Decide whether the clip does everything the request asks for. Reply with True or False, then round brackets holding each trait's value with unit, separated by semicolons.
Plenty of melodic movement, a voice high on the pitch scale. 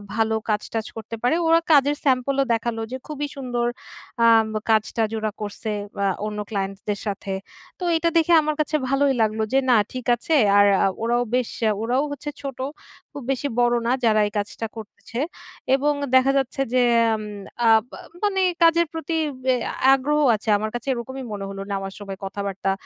False (4.3 semitones; 240 Hz)